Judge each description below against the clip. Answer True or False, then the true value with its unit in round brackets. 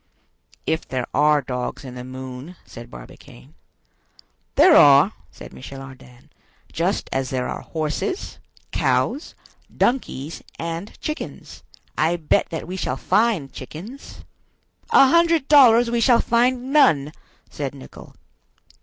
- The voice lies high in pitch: False (155 Hz)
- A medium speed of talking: False (125 wpm)